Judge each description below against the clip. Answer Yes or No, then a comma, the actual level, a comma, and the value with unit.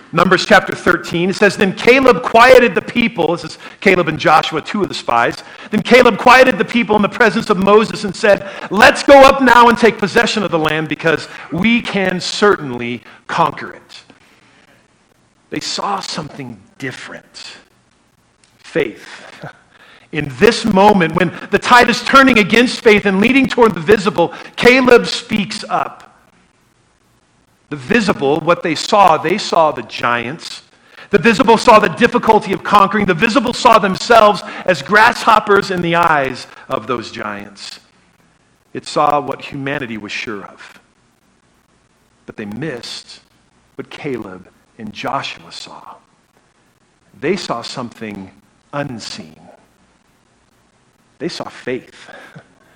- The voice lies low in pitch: No, high, 205 Hz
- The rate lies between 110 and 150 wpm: Yes, slow, 135 wpm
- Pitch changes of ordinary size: No, wide, 5.8 semitones